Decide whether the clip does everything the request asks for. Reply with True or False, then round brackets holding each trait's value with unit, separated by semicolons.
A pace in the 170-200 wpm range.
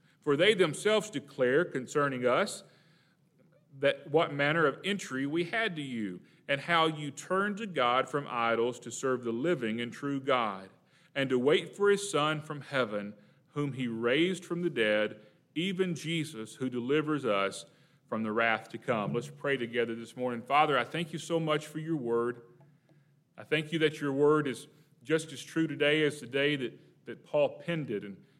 True (185 wpm)